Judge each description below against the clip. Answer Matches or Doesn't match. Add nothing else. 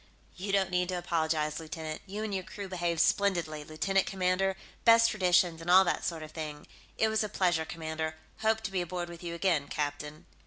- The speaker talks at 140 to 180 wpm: Doesn't match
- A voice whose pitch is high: Doesn't match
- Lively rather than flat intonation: Doesn't match